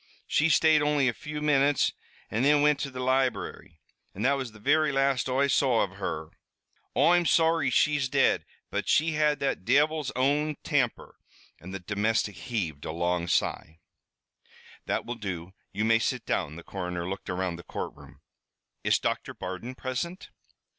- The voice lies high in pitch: No, low, 130 Hz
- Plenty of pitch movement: Yes, wide, 7.3 semitones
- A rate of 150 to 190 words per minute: Yes, average, 165 wpm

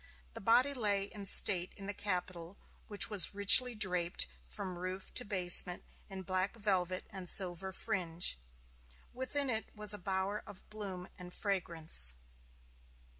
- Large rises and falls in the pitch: No, narrow, 2.5 semitones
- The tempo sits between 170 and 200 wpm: No, average, 140 wpm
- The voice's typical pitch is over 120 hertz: Yes, high, 190 Hz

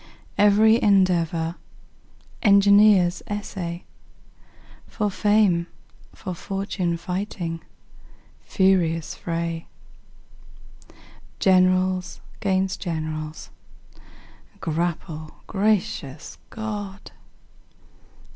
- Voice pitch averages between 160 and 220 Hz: Yes, medium, 185 Hz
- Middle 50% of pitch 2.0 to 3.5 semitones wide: Yes, average, 3.2 semitones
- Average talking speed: No, slow, 55 wpm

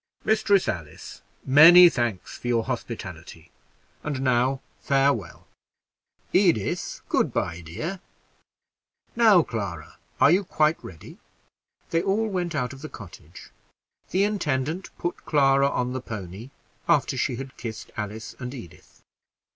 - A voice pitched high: No, low, 130 Hz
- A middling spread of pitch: No, wide, 7.4 semitones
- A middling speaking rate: No, slow, 125 wpm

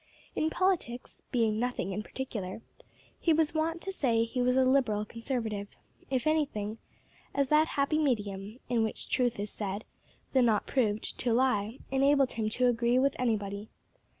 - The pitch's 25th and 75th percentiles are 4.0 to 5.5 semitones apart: Yes, average, 4.3 semitones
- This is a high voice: Yes, high, 245 Hz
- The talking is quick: No, average, 160 wpm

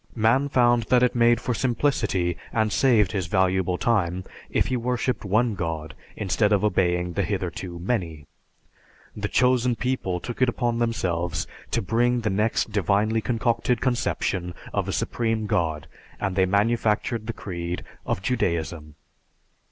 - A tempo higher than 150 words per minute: No, average, 145 wpm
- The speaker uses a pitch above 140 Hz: No, low, 105 Hz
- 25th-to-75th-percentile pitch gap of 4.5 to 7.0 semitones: Yes, average, 4.9 semitones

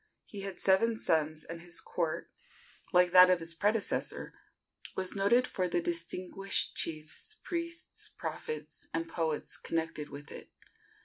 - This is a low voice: No, medium, 180 Hz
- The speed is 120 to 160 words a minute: Yes, slow, 135 wpm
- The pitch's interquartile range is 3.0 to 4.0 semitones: Yes, average, 3.5 semitones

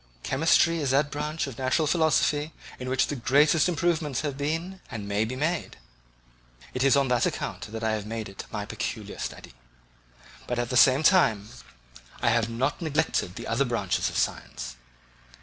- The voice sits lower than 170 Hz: Yes, low, 135 Hz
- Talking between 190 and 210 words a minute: No, average, 175 wpm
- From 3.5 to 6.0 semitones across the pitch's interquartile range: Yes, average, 5.1 semitones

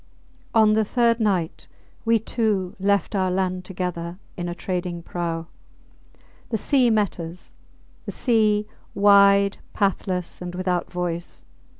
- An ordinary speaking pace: No, slow, 125 wpm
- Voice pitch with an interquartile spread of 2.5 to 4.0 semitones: Yes, average, 3.0 semitones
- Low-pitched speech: No, high, 190 Hz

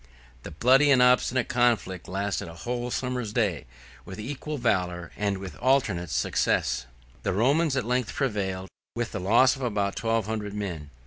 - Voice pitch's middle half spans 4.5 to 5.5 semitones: Yes, average, 4.8 semitones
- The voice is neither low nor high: No, low, 110 Hz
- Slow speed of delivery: No, average, 165 wpm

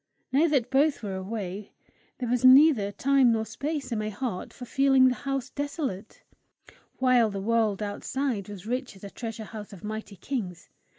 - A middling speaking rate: Yes, average, 175 wpm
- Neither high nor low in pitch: No, high, 230 Hz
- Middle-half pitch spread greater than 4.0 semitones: Yes, average, 4.6 semitones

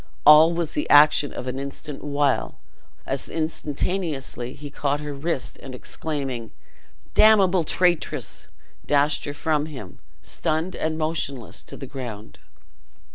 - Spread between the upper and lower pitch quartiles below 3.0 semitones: Yes, narrow, 2.6 semitones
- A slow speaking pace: Yes, slow, 130 wpm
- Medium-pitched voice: Yes, medium, 150 Hz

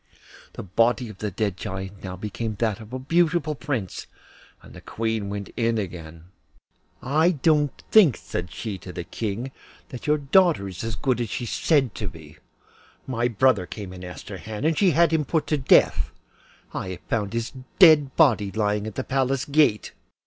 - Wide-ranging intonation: Yes, wide, 5.8 semitones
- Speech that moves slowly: No, average, 195 wpm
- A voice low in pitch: Yes, low, 115 Hz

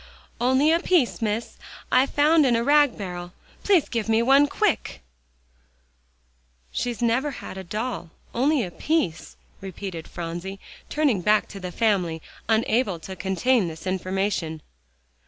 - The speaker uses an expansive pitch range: Yes, wide, 6.1 semitones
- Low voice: No, high, 220 Hz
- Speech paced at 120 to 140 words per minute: Yes, slow, 135 wpm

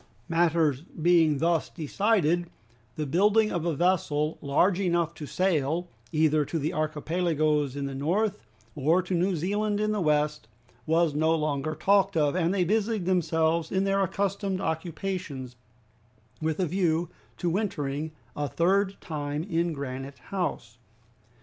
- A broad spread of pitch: No, average, 3.6 semitones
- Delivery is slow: No, average, 145 wpm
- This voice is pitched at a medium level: Yes, medium, 165 Hz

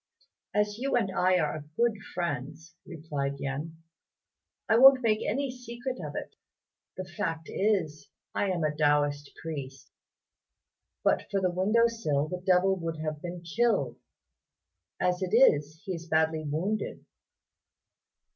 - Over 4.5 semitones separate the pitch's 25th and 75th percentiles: Yes, average, 5.3 semitones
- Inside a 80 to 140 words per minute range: Yes, slow, 135 wpm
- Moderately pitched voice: Yes, medium, 175 Hz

